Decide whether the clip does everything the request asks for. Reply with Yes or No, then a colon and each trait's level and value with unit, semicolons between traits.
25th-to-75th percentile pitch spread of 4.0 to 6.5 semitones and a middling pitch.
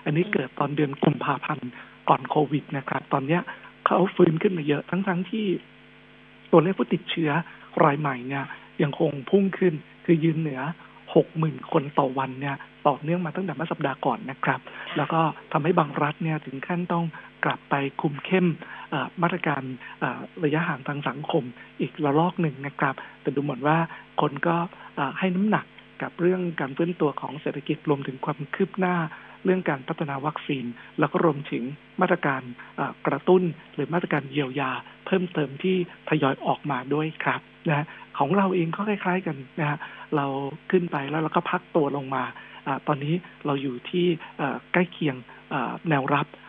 No: average, 3.6 semitones; medium, 155 Hz